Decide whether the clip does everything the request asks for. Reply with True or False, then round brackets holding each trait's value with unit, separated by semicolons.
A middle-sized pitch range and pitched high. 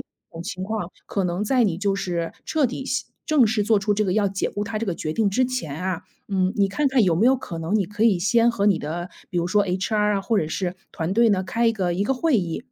True (3.9 semitones; 200 Hz)